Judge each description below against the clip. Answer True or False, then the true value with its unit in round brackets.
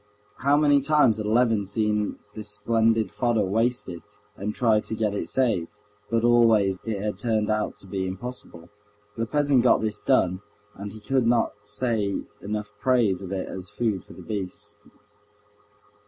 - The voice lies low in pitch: True (110 Hz)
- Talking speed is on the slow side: False (170 wpm)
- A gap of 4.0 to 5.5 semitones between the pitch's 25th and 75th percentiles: False (2.8 semitones)